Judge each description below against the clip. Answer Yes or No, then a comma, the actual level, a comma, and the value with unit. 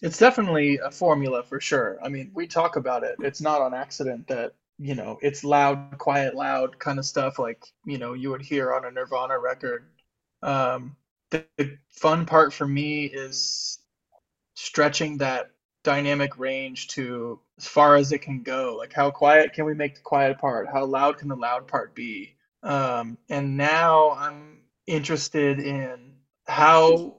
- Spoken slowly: No, average, 170 wpm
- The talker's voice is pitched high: No, medium, 140 Hz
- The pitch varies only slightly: Yes, narrow, 2.0 semitones